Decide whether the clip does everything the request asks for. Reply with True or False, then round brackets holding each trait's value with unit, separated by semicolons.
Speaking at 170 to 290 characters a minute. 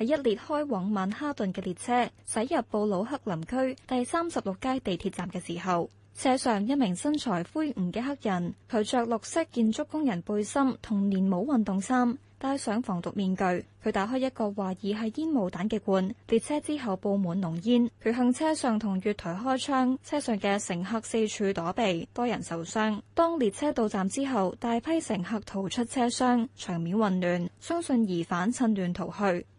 True (270 characters per minute)